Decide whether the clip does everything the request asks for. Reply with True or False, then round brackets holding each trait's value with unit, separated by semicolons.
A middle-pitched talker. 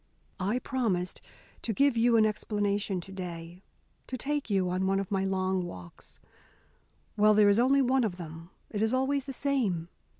False (205 Hz)